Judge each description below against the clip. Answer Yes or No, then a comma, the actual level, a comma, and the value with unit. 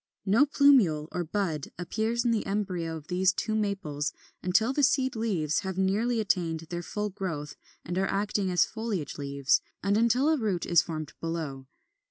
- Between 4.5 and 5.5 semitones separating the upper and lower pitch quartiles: Yes, average, 5.1 semitones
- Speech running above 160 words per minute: Yes, average, 175 wpm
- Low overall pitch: No, high, 190 Hz